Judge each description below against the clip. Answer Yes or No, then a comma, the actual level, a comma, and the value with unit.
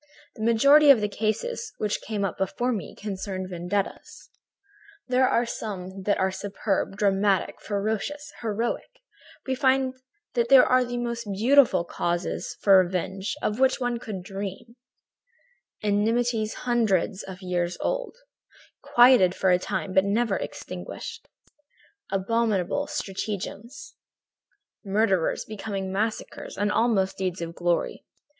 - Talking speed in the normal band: No, slow, 120 wpm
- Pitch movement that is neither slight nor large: Yes, average, 3.9 semitones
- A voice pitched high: Yes, high, 210 Hz